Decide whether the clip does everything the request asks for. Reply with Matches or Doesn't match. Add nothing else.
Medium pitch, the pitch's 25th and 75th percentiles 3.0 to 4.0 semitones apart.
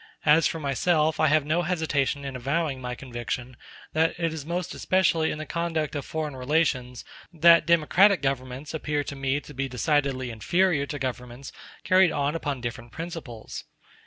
Matches